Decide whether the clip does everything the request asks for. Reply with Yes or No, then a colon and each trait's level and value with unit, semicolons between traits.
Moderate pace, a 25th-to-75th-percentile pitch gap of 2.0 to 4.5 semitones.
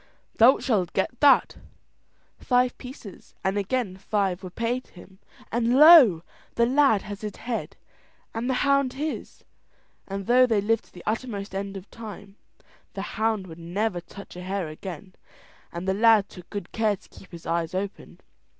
Yes: average, 175 wpm; average, 4.0 semitones